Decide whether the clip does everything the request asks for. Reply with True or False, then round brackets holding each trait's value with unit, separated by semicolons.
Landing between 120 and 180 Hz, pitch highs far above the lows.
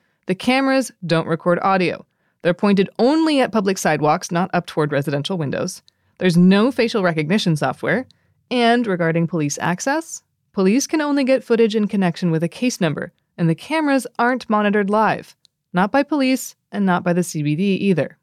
False (190 Hz; 6.1 semitones)